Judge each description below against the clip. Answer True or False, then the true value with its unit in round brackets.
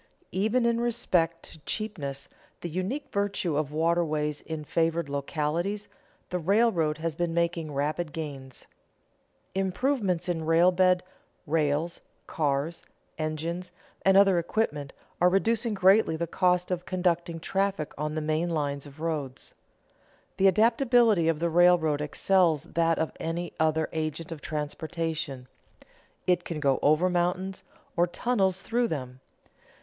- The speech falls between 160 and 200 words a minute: False (135 wpm)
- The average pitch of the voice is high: False (170 Hz)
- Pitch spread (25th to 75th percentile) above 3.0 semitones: True (3.4 semitones)